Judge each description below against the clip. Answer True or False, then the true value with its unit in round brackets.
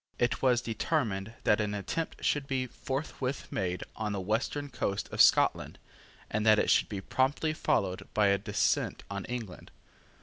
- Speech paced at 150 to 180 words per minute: True (165 wpm)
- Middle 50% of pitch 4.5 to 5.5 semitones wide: True (4.8 semitones)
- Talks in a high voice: False (110 Hz)